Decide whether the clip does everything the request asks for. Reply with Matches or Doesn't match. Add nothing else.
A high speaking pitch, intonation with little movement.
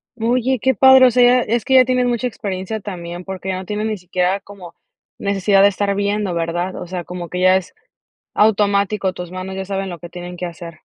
Doesn't match